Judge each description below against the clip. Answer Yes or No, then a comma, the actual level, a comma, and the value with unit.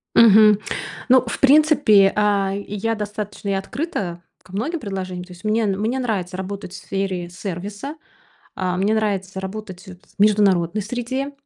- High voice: Yes, high, 205 Hz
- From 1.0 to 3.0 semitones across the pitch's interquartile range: Yes, narrow, 2.6 semitones